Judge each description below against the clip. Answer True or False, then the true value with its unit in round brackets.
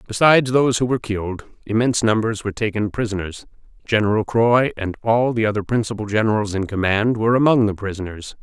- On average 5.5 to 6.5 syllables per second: True (6.3 syllables/s)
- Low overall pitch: True (110 Hz)